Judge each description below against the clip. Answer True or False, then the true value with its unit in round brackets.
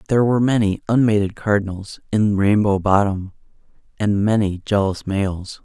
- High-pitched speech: False (105 Hz)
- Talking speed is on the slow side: True (130 wpm)